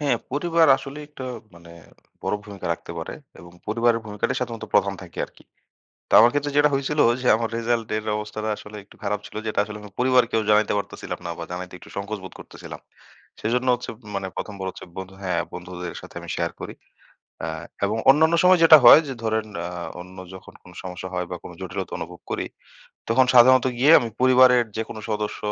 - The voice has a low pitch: Yes, low, 110 Hz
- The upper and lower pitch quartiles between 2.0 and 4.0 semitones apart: No, average, 5.1 semitones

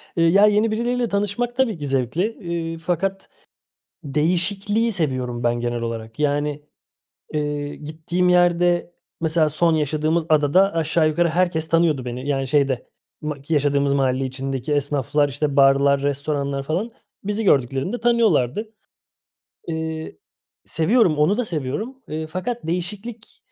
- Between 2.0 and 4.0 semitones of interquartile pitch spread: No, average, 4.6 semitones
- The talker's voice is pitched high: No, medium, 155 Hz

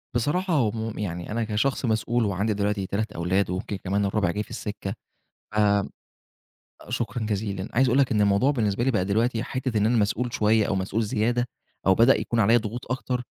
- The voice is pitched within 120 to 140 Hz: No, low, 110 Hz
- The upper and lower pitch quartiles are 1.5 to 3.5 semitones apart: Yes, average, 3.0 semitones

